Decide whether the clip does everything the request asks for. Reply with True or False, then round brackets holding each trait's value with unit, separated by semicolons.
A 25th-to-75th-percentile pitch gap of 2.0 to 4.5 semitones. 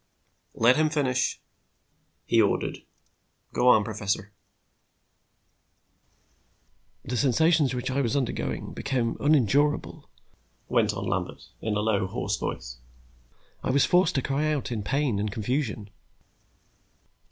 False (5.1 semitones)